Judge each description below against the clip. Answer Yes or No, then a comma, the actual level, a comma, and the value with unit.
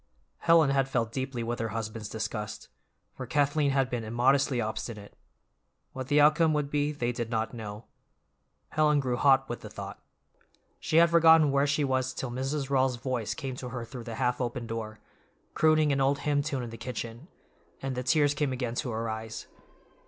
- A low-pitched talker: Yes, low, 130 Hz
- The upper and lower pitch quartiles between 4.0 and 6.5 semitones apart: No, average, 3.5 semitones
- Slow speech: No, average, 190 wpm